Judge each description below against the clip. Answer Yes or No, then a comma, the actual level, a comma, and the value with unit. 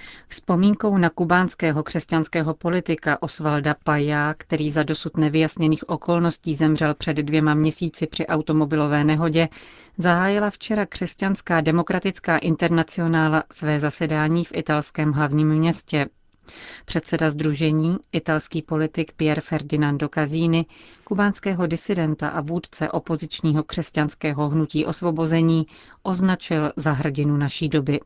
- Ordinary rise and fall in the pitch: No, narrow, 1.7 semitones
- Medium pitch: Yes, medium, 160 Hz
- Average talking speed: No, slow, 105 wpm